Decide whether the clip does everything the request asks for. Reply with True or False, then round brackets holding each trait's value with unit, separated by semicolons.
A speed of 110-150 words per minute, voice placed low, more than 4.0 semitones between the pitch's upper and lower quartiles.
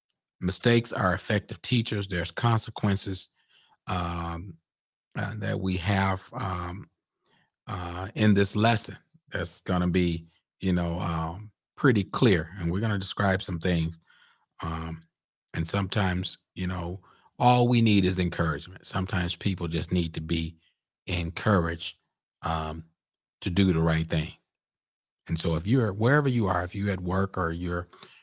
False (140 wpm; 95 Hz; 3.3 semitones)